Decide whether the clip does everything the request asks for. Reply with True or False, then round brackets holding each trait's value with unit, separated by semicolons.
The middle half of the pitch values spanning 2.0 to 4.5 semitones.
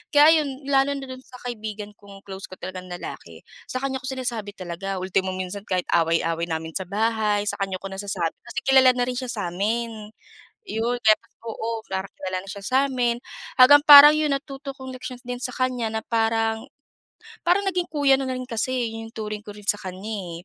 False (4.9 semitones)